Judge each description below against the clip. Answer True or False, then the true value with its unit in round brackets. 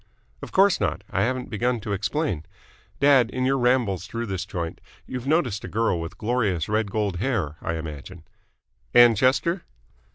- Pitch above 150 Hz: False (110 Hz)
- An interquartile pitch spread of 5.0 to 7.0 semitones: True (5.5 semitones)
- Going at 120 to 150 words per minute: False (165 wpm)